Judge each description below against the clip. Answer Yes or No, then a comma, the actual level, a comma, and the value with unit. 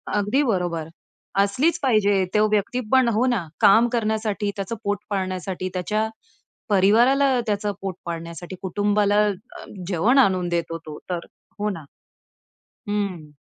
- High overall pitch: Yes, high, 205 Hz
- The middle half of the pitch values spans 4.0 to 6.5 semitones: No, average, 3.1 semitones